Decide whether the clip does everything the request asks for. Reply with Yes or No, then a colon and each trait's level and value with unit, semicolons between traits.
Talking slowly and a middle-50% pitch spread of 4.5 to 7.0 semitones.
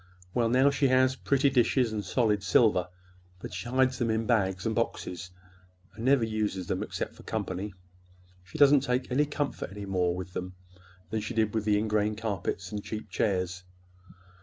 No: average, 170 wpm; average, 4.9 semitones